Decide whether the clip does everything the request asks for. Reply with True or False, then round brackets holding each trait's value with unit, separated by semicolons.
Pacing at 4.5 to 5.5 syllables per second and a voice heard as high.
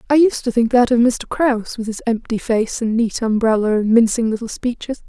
True (5.4 syllables/s; 235 Hz)